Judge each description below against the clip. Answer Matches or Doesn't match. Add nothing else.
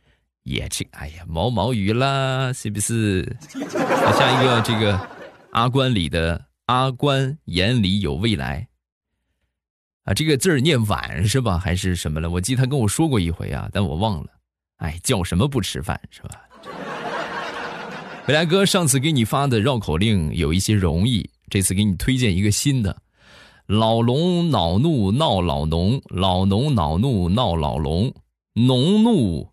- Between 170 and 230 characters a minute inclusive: Matches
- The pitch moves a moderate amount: Doesn't match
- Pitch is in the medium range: Doesn't match